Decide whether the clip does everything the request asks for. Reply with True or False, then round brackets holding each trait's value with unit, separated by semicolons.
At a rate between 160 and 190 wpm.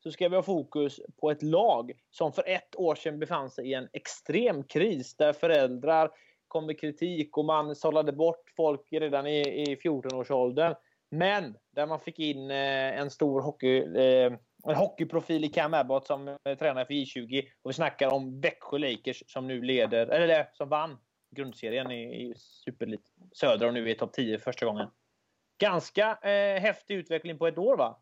True (180 wpm)